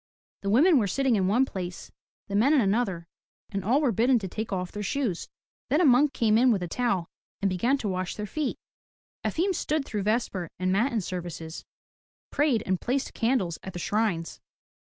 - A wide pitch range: Yes, wide, 5.7 semitones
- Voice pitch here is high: Yes, high, 215 Hz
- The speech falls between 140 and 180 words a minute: No, average, 195 wpm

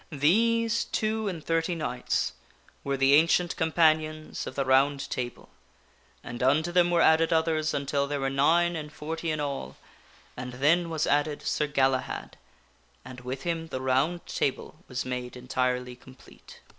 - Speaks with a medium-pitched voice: Yes, medium, 150 Hz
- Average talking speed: Yes, average, 155 wpm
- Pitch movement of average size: Yes, average, 3.7 semitones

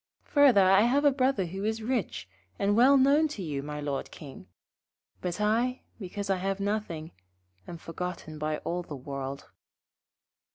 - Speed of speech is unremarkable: Yes, average, 160 wpm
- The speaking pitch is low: No, high, 195 Hz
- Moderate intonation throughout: No, wide, 7.1 semitones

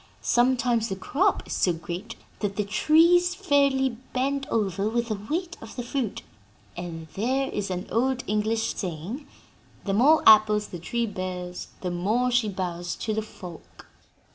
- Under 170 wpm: Yes, average, 160 wpm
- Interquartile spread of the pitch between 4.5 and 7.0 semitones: Yes, wide, 5.6 semitones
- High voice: Yes, high, 220 Hz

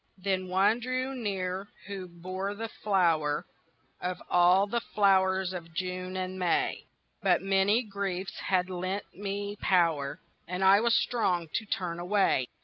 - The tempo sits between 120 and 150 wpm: Yes, average, 145 wpm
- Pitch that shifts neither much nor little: No, narrow, 1.9 semitones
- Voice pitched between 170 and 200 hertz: Yes, high, 190 Hz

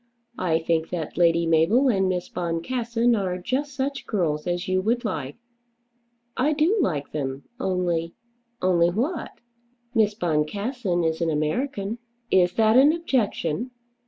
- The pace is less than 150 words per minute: Yes, average, 140 wpm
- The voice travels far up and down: Yes, wide, 6.4 semitones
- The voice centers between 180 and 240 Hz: Yes, medium, 185 Hz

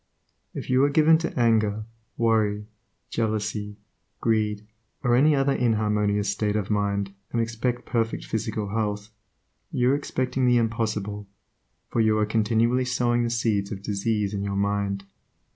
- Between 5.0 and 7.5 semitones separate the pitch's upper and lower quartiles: No, narrow, 2.5 semitones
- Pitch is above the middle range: No, low, 110 Hz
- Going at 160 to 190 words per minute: No, average, 145 wpm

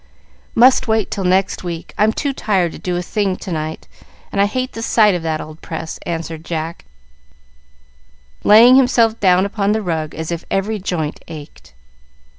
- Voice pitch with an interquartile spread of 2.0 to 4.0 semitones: No, average, 4.9 semitones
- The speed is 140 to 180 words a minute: Yes, average, 175 wpm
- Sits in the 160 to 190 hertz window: Yes, medium, 185 Hz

